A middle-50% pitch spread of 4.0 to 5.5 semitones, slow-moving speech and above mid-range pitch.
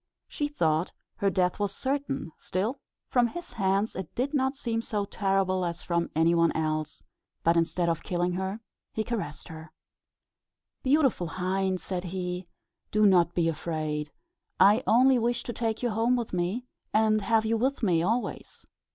No: average, 5.1 semitones; average, 165 wpm; high, 195 Hz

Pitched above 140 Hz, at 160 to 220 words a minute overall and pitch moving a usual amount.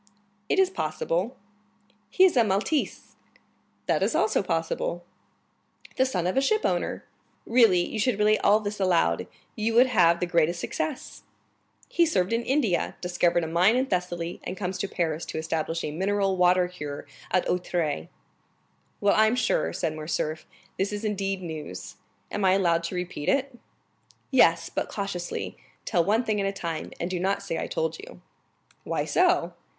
Yes: medium, 185 Hz; average, 165 wpm; average, 4.2 semitones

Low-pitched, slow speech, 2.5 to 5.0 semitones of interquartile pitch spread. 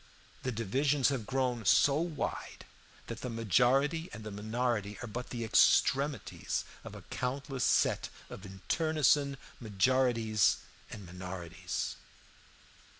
Yes: low, 125 Hz; slow, 115 wpm; average, 4.3 semitones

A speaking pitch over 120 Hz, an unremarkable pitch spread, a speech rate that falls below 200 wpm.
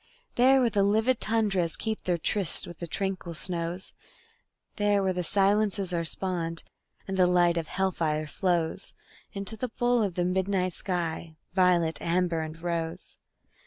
Yes: medium, 185 Hz; average, 3.0 semitones; average, 160 wpm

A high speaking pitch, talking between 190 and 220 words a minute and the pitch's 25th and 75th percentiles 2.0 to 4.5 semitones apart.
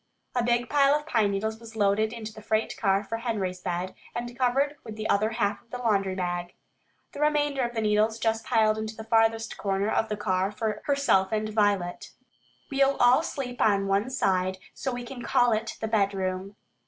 Yes: high, 220 Hz; average, 200 wpm; average, 3.3 semitones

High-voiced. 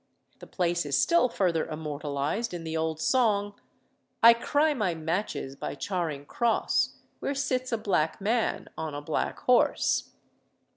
No: medium, 180 Hz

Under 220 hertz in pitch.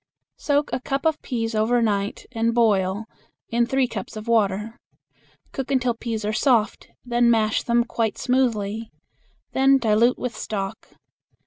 No: high, 230 Hz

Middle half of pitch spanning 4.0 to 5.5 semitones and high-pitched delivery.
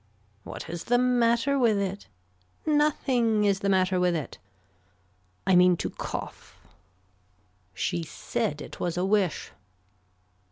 Yes: average, 4.9 semitones; high, 200 Hz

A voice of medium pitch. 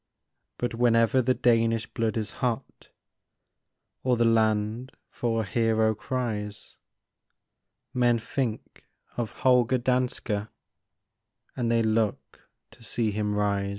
No: low, 115 Hz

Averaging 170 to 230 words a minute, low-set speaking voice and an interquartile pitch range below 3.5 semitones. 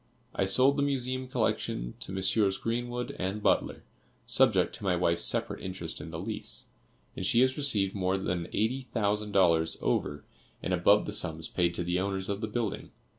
No: average, 180 wpm; very low, 95 Hz; average, 4.4 semitones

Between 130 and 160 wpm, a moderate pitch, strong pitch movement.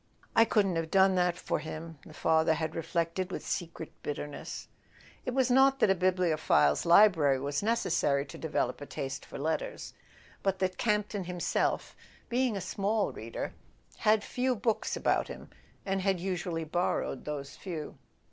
No: average, 155 wpm; medium, 175 Hz; average, 4.4 semitones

